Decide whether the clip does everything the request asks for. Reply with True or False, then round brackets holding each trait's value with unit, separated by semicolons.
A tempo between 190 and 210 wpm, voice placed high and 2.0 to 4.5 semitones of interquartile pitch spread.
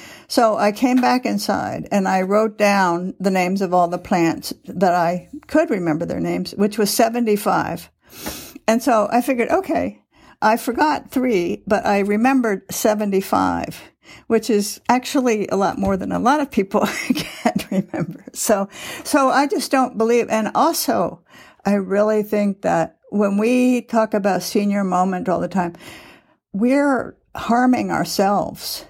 False (150 wpm; 215 Hz; 4.2 semitones)